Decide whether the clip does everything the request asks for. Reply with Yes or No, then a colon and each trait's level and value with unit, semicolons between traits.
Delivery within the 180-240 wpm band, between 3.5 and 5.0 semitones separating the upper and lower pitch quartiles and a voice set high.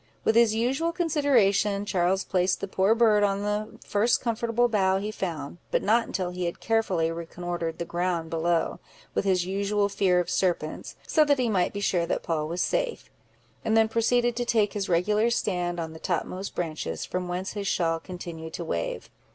Yes: average, 190 wpm; average, 4.0 semitones; high, 195 Hz